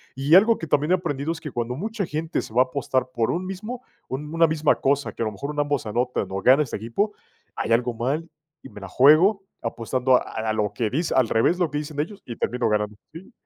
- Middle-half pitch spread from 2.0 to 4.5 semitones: No, wide, 5.6 semitones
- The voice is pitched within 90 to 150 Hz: Yes, medium, 140 Hz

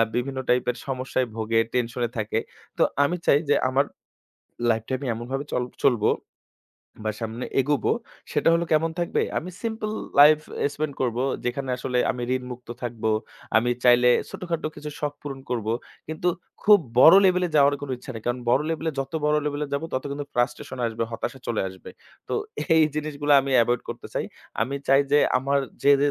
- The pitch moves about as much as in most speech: Yes, average, 3.4 semitones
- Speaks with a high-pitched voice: No, low, 135 Hz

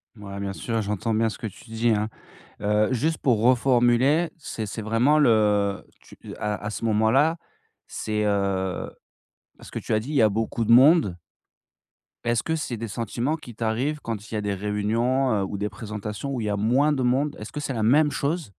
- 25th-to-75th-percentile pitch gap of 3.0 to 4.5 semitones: Yes, average, 3.9 semitones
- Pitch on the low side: Yes, low, 115 Hz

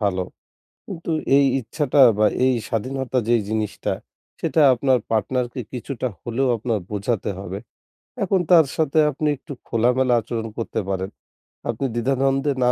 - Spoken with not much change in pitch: No, average, 3.5 semitones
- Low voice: Yes, low, 125 Hz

